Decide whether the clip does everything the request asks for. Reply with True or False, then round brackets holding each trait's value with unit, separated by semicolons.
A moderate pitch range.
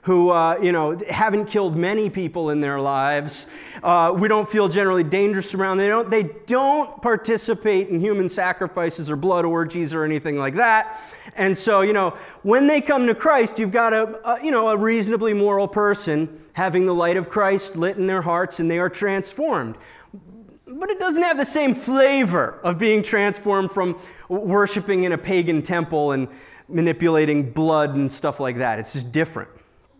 True (4.5 semitones)